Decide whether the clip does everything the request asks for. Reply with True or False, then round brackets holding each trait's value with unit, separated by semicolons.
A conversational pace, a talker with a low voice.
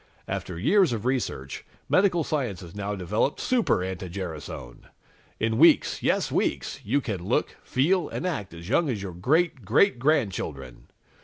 True (155 wpm; 110 Hz)